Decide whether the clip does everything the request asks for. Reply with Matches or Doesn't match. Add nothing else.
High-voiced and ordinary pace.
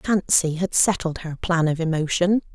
Doesn't match